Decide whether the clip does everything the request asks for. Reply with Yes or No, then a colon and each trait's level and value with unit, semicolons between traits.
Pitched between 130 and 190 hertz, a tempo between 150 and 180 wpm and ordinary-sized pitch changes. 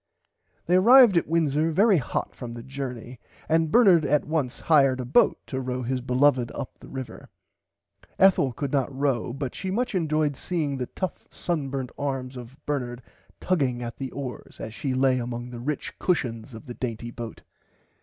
Yes: low, 135 Hz; average, 175 wpm; average, 3.9 semitones